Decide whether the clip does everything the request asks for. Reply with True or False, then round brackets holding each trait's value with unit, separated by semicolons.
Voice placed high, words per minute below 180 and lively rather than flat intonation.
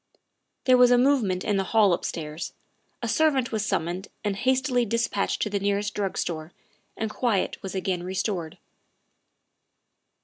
False (205 Hz; 160 wpm; 4.2 semitones)